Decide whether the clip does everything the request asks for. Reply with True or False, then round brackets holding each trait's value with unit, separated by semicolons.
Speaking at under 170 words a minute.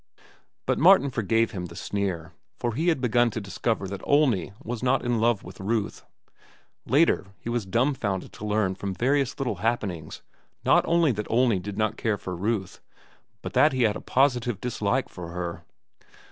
False (175 wpm)